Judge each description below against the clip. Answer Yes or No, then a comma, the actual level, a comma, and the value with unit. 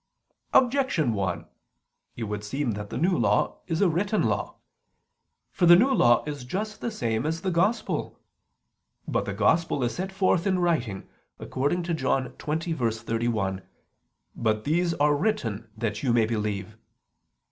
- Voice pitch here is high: No, medium, 145 Hz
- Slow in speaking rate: No, average, 150 wpm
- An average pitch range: No, wide, 7.8 semitones